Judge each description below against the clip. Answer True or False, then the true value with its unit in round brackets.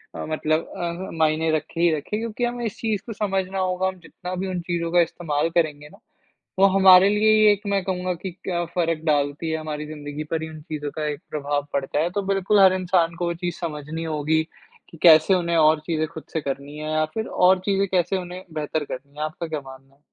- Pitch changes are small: False (3.5 semitones)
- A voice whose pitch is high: False (165 Hz)